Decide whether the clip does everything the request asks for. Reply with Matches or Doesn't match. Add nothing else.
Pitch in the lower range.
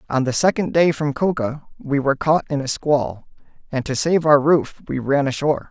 Doesn't match